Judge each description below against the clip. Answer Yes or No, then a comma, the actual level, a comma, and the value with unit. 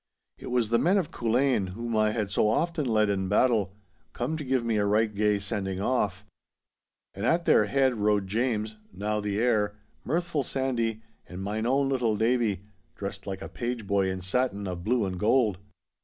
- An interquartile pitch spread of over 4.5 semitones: No, average, 3.6 semitones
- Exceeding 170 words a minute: Yes, average, 185 wpm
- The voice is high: No, low, 110 Hz